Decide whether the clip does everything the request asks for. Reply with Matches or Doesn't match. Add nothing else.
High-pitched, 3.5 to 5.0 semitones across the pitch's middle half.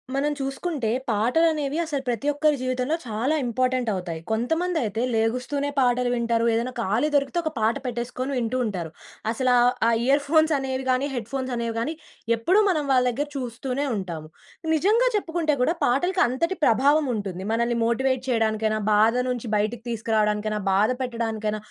Matches